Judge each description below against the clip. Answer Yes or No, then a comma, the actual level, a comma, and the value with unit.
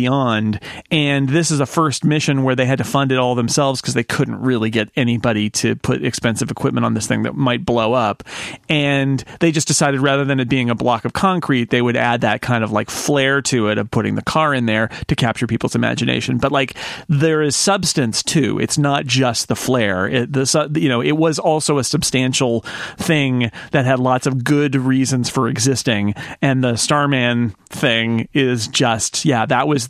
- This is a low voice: Yes, low, 130 Hz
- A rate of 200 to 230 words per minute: Yes, fast, 205 wpm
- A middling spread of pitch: Yes, average, 3.1 semitones